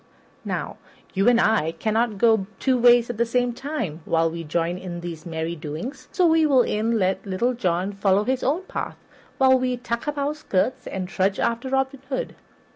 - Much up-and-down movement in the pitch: Yes, wide, 5.7 semitones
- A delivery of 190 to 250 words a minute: Yes, average, 195 wpm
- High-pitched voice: Yes, high, 230 Hz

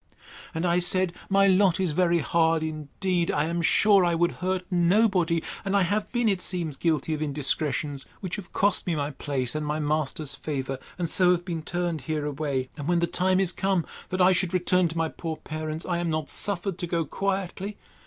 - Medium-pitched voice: Yes, medium, 170 Hz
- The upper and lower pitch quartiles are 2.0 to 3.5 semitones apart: Yes, average, 3.1 semitones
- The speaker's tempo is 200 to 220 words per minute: Yes, fast, 205 wpm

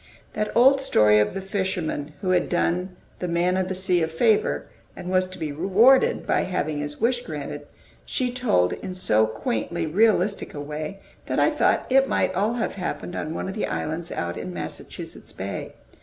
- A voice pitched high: No, medium, 180 Hz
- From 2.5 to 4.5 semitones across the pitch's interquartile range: No, average, 5.0 semitones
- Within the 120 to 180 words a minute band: No, average, 190 wpm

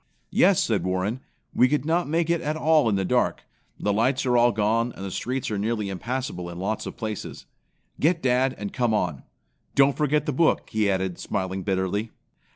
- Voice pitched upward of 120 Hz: No, low, 115 Hz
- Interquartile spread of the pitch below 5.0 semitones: No, wide, 5.6 semitones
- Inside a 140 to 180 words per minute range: No, average, 195 wpm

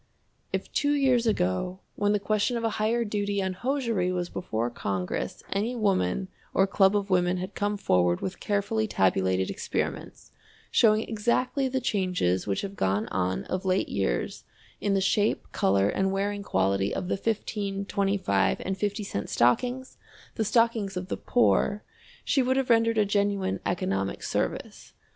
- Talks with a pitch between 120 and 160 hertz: No, high, 195 Hz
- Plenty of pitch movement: No, average, 3.6 semitones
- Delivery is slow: No, average, 160 wpm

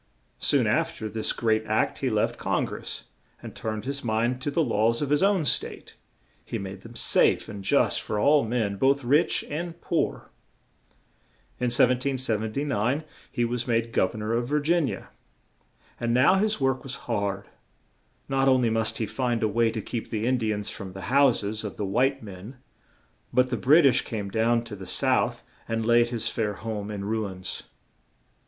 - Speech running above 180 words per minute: Yes, average, 190 wpm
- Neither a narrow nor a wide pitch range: Yes, average, 3.6 semitones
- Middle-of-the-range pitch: No, low, 115 Hz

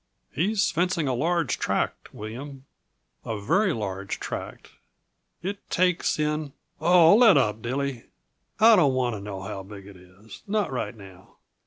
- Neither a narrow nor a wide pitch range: No, wide, 8.8 semitones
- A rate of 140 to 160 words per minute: Yes, average, 155 wpm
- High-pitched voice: No, low, 135 Hz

